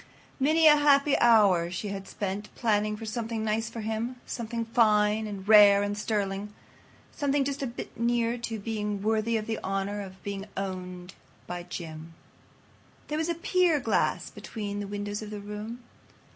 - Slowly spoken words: No, average, 170 wpm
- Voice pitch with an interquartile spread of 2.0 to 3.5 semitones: Yes, narrow, 2.6 semitones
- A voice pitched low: No, high, 215 Hz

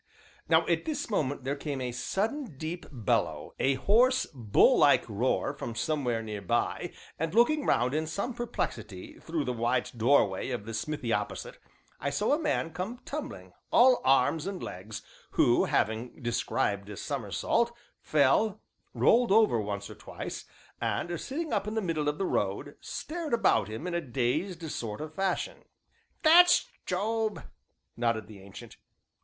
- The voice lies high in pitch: No, medium, 150 Hz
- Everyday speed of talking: Yes, average, 160 wpm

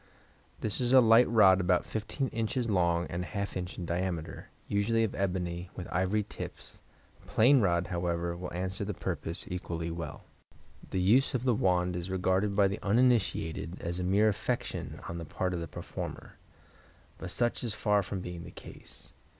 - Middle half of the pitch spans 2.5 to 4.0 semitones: Yes, average, 3.6 semitones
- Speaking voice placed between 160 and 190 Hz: No, very low, 95 Hz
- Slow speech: No, average, 180 wpm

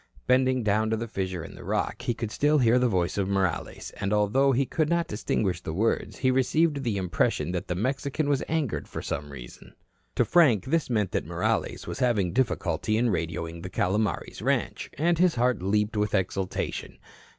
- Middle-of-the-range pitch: No, low, 110 Hz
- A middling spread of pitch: No, wide, 5.9 semitones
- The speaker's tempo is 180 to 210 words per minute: Yes, average, 195 wpm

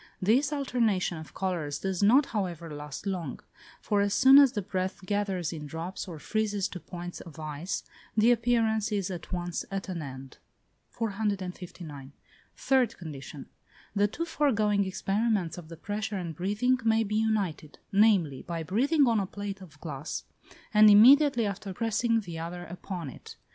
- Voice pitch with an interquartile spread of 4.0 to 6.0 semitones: Yes, average, 4.3 semitones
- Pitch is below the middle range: No, high, 195 Hz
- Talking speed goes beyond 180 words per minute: No, average, 160 wpm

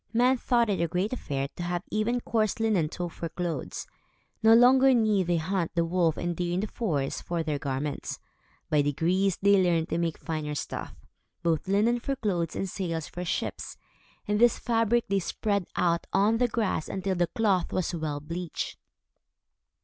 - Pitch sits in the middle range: Yes, medium, 180 Hz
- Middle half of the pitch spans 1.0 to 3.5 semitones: No, average, 4.6 semitones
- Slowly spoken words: No, average, 180 wpm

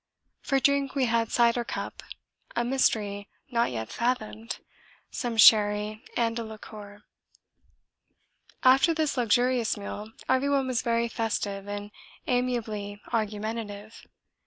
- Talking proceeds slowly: Yes, slow, 110 wpm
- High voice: Yes, high, 230 Hz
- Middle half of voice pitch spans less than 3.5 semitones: Yes, average, 3.0 semitones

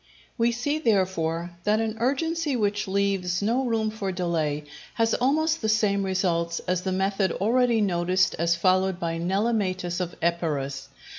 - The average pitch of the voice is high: Yes, high, 195 Hz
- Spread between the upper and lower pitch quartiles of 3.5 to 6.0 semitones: Yes, average, 4.4 semitones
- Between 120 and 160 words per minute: Yes, average, 150 wpm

